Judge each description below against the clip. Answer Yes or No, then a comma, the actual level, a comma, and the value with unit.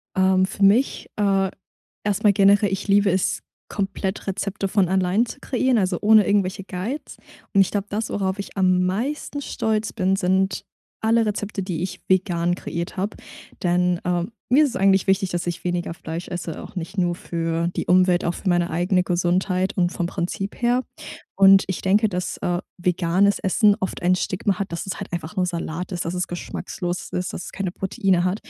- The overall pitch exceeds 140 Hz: Yes, high, 190 Hz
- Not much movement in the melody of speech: Yes, narrow, 2.1 semitones